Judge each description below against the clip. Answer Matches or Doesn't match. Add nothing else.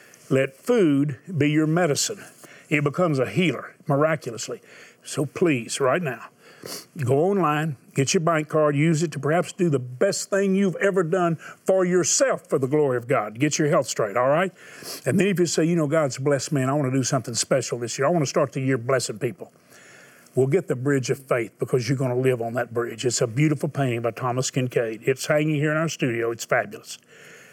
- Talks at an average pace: Doesn't match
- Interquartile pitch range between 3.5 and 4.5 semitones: Matches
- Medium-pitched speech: Matches